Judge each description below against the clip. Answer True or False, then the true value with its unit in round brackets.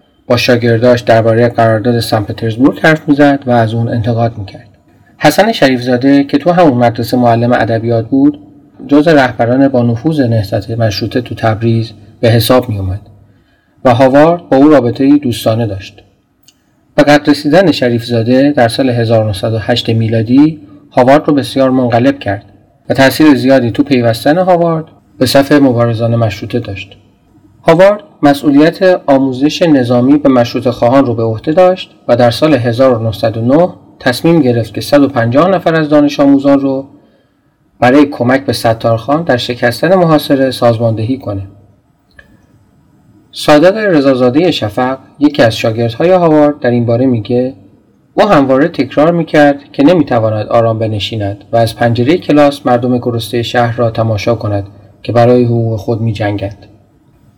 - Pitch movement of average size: True (3.8 semitones)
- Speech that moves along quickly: False (135 wpm)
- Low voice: True (125 Hz)